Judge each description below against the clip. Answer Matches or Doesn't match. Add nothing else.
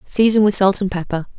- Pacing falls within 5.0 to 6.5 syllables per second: Matches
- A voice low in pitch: Doesn't match